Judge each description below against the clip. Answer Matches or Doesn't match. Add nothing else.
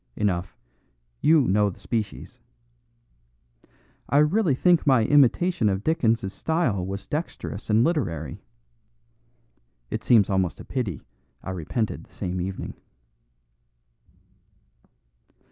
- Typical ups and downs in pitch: Doesn't match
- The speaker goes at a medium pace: Doesn't match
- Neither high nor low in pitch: Doesn't match